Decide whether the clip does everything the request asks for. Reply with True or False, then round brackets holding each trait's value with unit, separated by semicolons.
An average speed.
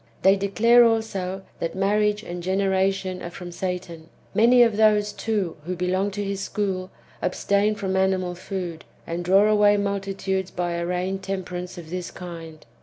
True (160 wpm)